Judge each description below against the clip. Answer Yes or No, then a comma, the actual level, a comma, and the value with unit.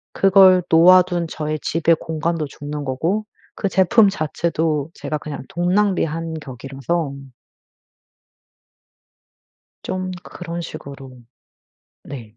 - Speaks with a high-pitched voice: No, medium, 165 Hz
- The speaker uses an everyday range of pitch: Yes, average, 3.6 semitones